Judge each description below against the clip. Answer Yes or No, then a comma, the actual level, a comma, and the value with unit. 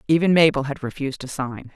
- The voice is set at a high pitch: No, medium, 140 Hz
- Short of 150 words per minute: No, fast, 205 wpm